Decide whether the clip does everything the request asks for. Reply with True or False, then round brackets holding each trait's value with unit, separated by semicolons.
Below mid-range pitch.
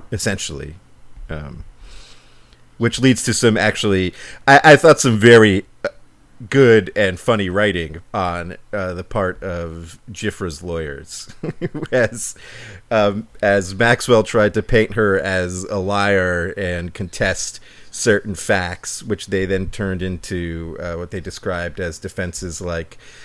True (100 Hz)